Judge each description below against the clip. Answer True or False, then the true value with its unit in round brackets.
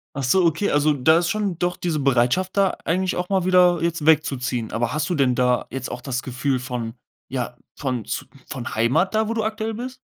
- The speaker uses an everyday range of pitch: False (6.6 semitones)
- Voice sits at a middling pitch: True (155 Hz)